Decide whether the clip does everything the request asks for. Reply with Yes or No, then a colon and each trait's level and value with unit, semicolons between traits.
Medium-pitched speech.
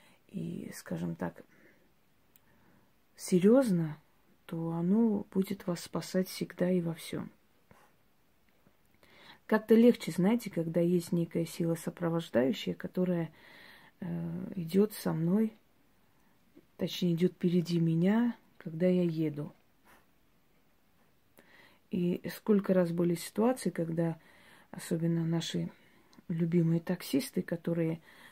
Yes: medium, 175 Hz